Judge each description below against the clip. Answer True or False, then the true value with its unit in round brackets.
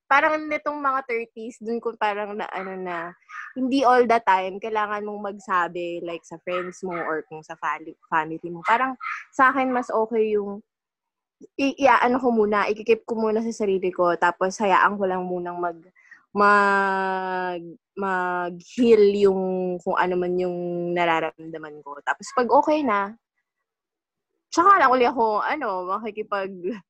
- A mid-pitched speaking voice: False (200 Hz)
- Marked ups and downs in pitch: False (4.5 semitones)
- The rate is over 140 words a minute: True (150 wpm)